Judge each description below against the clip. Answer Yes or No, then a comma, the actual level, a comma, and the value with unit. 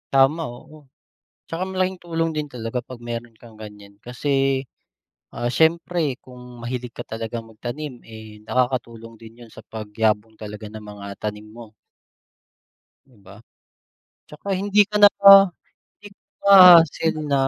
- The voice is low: Yes, low, 120 Hz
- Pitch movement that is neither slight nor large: No, wide, 5.7 semitones